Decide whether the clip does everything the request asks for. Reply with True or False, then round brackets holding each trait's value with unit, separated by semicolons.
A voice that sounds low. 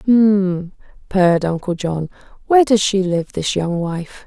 False (190 Hz)